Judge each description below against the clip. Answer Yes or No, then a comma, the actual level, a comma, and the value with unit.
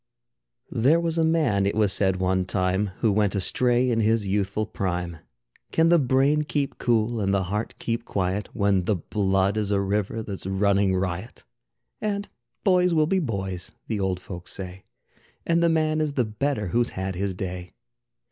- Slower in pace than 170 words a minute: No, average, 175 wpm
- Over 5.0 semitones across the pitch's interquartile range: Yes, wide, 5.5 semitones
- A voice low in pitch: Yes, low, 105 Hz